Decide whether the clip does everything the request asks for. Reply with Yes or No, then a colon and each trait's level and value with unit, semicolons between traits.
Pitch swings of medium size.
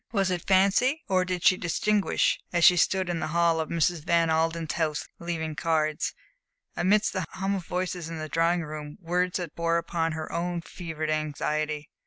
No: narrow, 2.3 semitones